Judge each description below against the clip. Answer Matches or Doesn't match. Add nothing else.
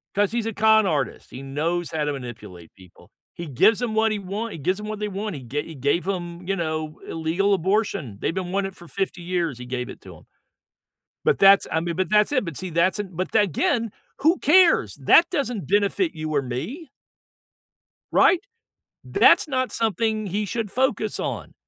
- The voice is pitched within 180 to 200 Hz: Matches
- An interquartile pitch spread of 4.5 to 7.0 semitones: Matches